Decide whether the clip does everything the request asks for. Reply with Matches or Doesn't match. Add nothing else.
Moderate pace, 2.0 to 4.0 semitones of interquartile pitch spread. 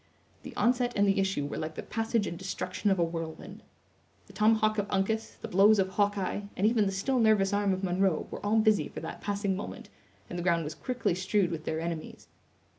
Doesn't match